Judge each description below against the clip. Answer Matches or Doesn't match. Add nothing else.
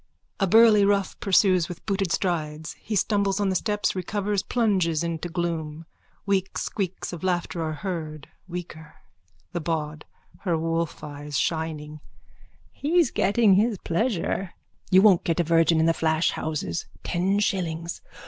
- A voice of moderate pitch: Matches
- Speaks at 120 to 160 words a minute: Matches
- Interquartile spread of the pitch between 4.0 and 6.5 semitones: Doesn't match